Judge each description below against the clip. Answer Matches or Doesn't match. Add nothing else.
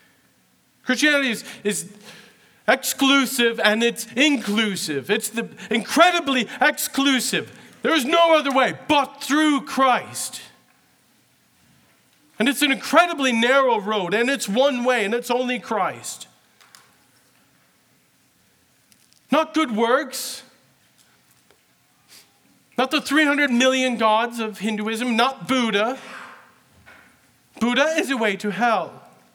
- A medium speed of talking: Doesn't match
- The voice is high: Matches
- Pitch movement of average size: Matches